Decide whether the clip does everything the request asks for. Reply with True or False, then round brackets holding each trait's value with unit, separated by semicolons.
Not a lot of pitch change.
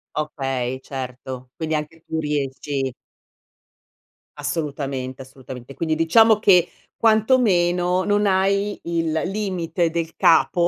False (5.3 semitones)